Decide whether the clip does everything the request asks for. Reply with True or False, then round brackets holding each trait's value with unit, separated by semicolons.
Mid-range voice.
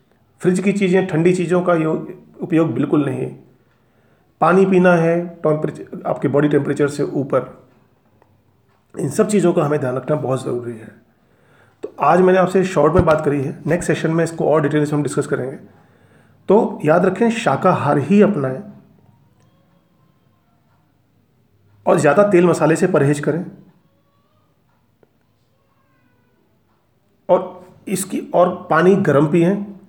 True (150 Hz)